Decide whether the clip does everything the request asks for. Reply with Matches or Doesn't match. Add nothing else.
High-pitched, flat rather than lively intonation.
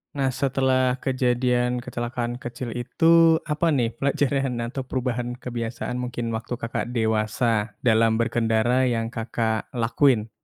Doesn't match